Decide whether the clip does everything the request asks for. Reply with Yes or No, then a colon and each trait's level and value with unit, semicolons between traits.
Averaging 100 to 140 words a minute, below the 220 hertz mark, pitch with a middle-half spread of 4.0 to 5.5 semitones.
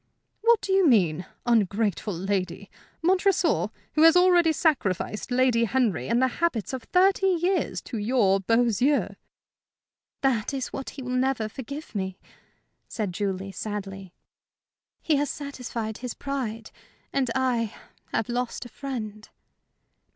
No: slow, 135 wpm; high, 245 Hz; average, 5.2 semitones